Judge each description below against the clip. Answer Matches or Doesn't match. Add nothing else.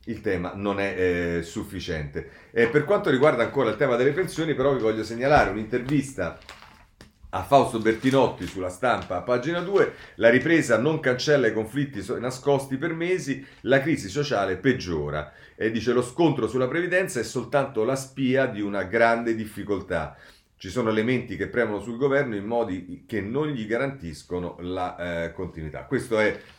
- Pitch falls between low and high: Doesn't match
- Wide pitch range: Matches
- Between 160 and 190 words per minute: Matches